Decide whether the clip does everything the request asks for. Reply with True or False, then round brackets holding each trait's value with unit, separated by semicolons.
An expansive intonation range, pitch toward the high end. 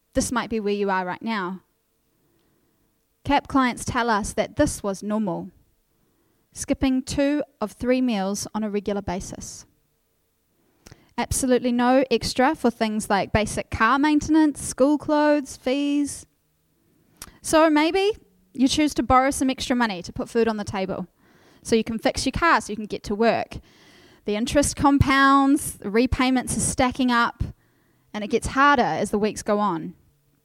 False (4.7 semitones; 245 Hz)